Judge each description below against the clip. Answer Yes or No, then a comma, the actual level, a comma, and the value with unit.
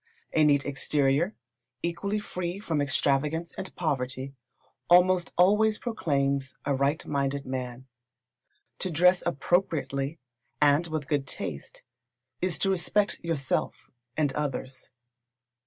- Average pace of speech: No, slow, 110 wpm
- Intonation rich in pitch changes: No, average, 4.3 semitones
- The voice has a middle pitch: Yes, medium, 150 Hz